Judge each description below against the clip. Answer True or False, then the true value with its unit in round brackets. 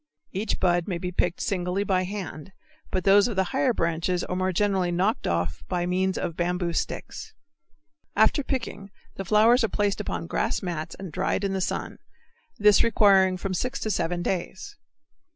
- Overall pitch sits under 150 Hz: False (185 Hz)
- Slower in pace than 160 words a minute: False (175 wpm)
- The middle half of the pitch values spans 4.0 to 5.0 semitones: False (2.7 semitones)